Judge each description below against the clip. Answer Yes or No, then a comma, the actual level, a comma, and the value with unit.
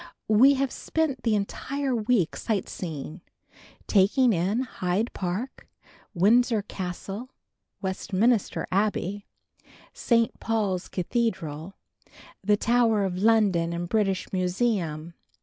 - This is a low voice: No, high, 205 Hz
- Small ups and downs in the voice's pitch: No, average, 4.4 semitones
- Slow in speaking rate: Yes, slow, 95 wpm